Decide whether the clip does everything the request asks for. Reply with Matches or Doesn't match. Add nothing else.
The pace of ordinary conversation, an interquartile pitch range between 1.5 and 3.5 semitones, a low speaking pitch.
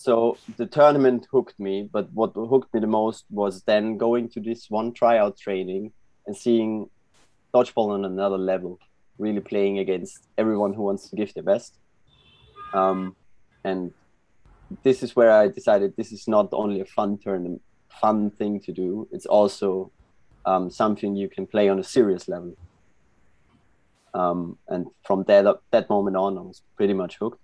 Matches